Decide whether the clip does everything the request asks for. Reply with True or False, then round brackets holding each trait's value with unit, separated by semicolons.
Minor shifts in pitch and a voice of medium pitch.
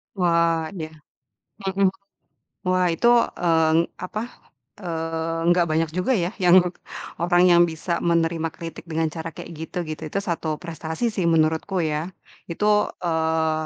True (2.0 semitones; 170 Hz)